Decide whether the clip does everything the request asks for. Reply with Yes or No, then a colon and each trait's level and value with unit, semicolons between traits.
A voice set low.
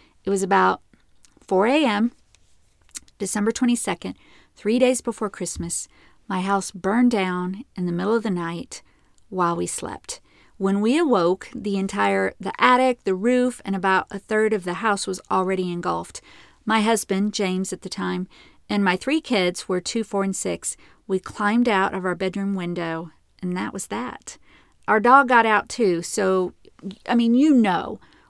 No: high, 195 Hz